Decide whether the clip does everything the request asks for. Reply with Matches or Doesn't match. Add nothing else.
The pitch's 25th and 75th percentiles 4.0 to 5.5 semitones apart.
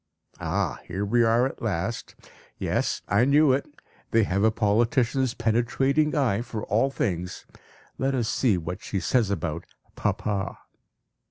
Matches